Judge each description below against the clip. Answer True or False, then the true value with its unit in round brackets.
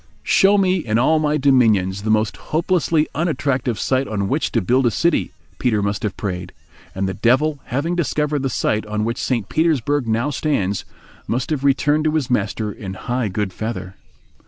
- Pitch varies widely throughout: True (5.9 semitones)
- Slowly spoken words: False (180 wpm)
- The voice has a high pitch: False (125 Hz)